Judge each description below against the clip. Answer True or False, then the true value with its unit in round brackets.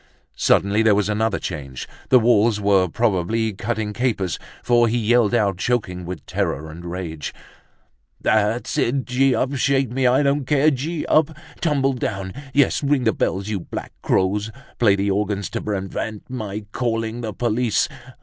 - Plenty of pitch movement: False (4.1 semitones)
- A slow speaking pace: False (160 wpm)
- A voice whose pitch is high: False (110 Hz)